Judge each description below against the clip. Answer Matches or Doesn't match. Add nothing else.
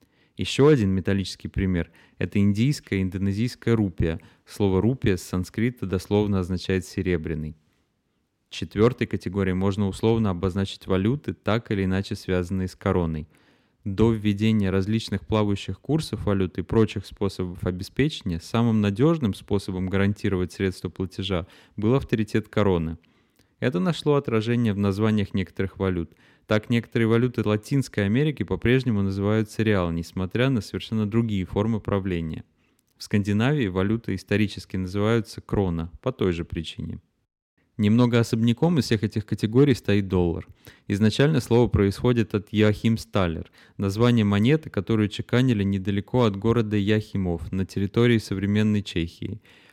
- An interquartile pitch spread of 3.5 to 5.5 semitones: Doesn't match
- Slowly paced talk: Doesn't match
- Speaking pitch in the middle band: Doesn't match